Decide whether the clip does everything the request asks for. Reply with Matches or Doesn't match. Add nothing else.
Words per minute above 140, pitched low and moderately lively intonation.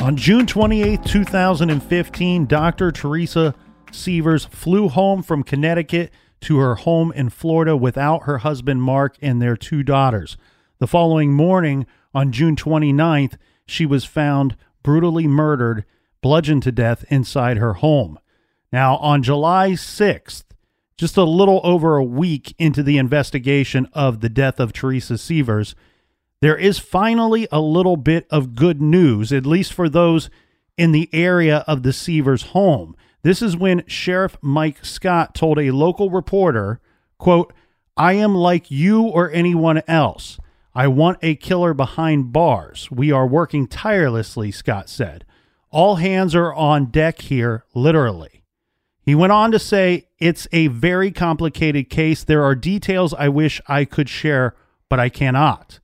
Doesn't match